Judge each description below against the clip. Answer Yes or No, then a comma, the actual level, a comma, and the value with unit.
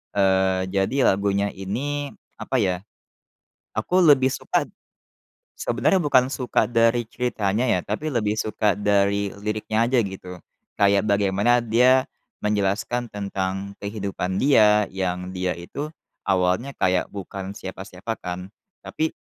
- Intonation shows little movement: No, average, 3.8 semitones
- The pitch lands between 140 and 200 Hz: No, low, 100 Hz